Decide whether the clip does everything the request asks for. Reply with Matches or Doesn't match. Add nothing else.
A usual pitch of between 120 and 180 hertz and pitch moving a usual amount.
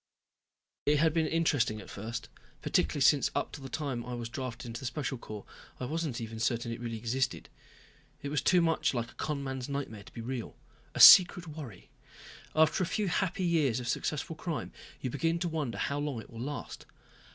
Matches